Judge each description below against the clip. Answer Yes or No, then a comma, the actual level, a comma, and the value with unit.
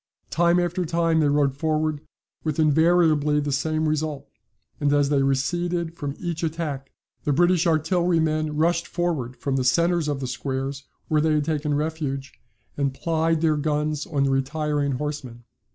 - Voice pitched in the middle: Yes, medium, 155 Hz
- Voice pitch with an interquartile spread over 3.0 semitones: No, narrow, 2.5 semitones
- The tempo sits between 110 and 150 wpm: No, average, 160 wpm